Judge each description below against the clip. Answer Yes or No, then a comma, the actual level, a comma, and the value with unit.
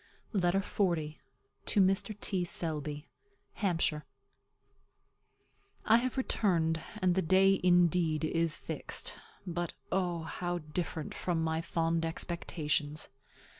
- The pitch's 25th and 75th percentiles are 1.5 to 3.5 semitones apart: Yes, average, 2.7 semitones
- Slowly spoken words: Yes, slow, 105 wpm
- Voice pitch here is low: No, medium, 170 Hz